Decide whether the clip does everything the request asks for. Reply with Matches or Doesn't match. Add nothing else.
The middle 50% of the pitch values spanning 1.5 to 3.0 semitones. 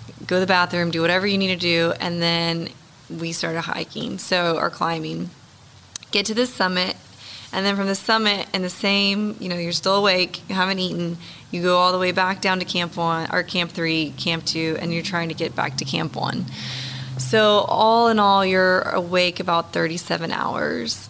Matches